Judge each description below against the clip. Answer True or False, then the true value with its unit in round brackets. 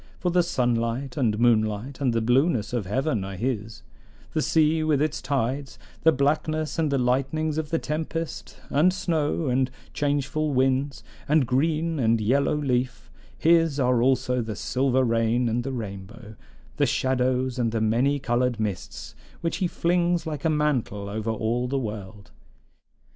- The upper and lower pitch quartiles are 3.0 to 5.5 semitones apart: True (4.6 semitones)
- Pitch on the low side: True (130 Hz)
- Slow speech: False (160 wpm)